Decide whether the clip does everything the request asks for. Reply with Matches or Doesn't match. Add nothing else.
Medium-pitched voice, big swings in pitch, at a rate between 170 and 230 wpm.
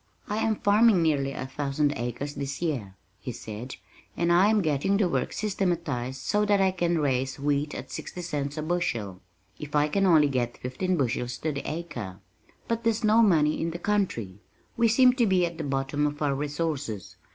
Matches